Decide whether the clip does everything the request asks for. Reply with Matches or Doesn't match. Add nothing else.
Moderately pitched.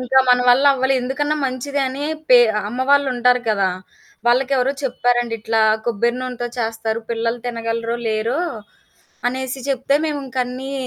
Doesn't match